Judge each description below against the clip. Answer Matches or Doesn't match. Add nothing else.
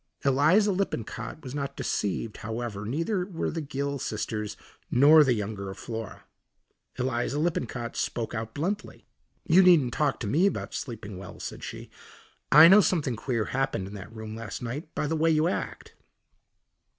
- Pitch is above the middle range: Doesn't match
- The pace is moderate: Matches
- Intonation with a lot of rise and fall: Matches